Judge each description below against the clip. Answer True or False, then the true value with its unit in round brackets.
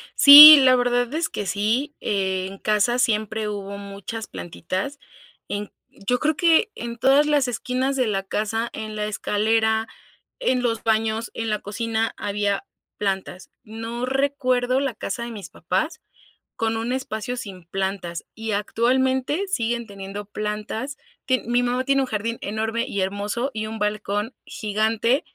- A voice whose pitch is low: False (225 Hz)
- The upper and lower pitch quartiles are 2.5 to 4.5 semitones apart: True (3.4 semitones)